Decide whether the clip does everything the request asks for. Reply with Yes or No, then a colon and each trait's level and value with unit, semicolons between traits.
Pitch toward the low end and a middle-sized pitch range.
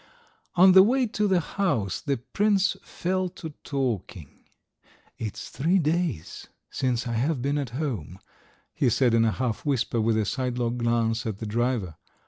No: low, 125 Hz; wide, 6.9 semitones